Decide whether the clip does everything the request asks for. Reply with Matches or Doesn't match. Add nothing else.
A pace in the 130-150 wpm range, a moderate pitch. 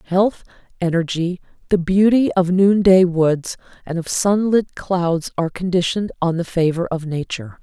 Matches